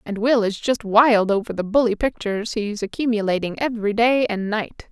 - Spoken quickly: No, average, 185 wpm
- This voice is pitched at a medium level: No, high, 220 Hz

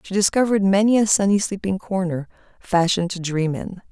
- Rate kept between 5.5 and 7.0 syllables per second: Yes, 5.9 syllables/s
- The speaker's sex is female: Yes, female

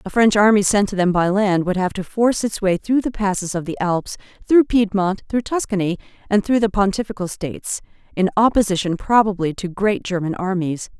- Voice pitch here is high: Yes, high, 200 Hz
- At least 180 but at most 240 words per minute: Yes, average, 195 wpm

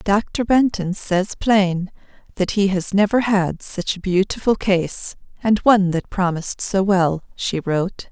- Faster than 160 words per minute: No, average, 155 wpm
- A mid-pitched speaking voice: No, high, 195 Hz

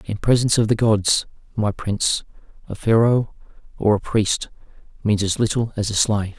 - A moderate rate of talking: Yes, average, 170 wpm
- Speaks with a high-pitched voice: No, low, 110 Hz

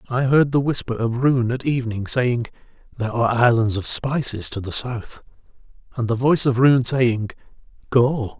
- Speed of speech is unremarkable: Yes, average, 170 wpm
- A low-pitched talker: Yes, low, 120 Hz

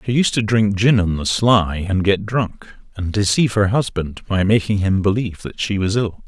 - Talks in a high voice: No, low, 100 Hz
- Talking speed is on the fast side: Yes, fast, 220 wpm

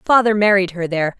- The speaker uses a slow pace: No, average, 200 wpm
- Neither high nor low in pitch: No, high, 195 Hz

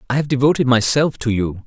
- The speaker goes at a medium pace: No, fast, 215 wpm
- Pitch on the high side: No, low, 125 Hz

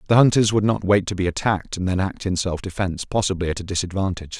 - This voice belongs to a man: Yes, male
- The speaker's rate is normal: No, fast, 245 wpm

